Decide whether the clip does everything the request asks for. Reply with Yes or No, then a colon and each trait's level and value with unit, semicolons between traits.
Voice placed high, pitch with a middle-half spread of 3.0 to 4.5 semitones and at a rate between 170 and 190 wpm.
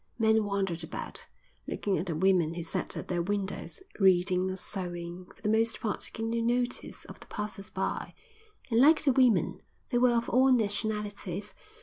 Yes: high, 205 Hz; average, 3.8 semitones; average, 180 wpm